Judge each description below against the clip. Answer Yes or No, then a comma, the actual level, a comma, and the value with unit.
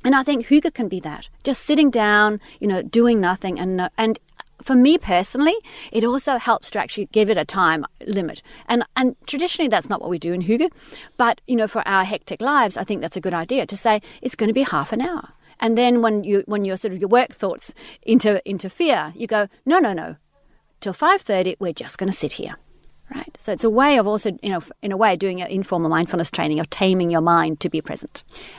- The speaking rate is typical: No, fast, 235 wpm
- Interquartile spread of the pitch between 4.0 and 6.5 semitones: Yes, average, 5.1 semitones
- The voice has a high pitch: Yes, high, 215 Hz